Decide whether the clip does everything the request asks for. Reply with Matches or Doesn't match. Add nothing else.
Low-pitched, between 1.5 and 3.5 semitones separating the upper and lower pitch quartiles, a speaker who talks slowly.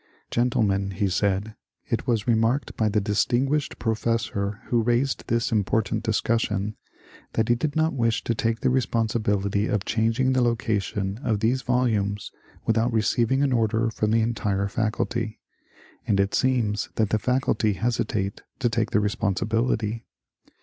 Doesn't match